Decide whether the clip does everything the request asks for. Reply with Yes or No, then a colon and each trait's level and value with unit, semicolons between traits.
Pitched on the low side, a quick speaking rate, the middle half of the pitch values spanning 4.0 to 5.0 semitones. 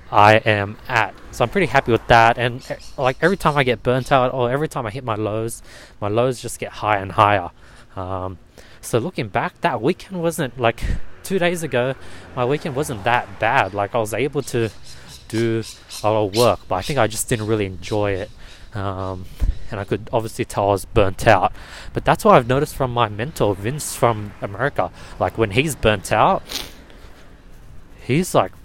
No: low, 115 Hz; average, 195 wpm; average, 4.4 semitones